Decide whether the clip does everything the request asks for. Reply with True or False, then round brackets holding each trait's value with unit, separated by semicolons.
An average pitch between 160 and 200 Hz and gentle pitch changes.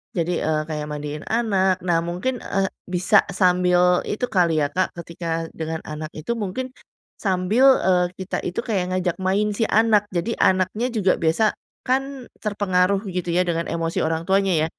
False (185 Hz; 3.6 semitones)